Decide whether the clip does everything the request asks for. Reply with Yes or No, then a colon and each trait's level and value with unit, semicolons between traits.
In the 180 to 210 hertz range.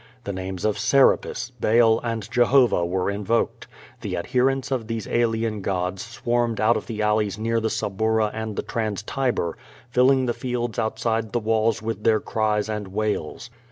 No: low, 110 Hz